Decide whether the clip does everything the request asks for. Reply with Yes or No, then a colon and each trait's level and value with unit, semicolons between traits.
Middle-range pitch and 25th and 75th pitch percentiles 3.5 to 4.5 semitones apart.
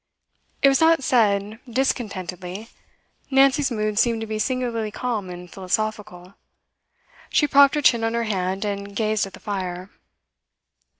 No: high, 215 Hz; average, 4.0 semitones